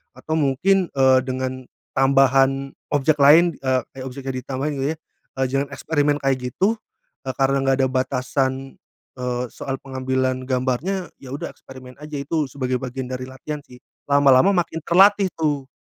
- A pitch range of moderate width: No, narrow, 2.1 semitones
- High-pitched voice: No, low, 135 Hz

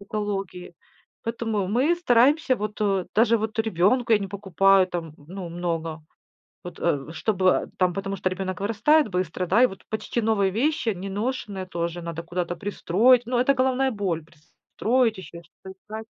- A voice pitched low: No, high, 195 Hz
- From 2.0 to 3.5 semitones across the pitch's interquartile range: No, average, 4.1 semitones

